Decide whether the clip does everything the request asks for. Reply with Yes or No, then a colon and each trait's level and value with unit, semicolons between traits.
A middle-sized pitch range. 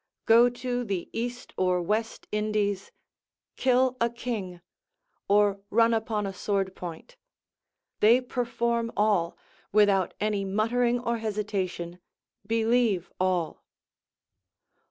Yes: average, 3.4 semitones